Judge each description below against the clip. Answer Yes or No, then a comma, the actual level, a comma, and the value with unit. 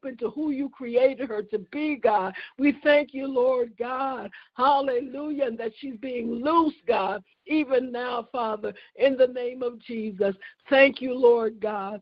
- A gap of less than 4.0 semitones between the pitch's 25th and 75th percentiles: Yes, average, 2.8 semitones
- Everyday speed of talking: Yes, average, 160 wpm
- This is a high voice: Yes, very high, 255 Hz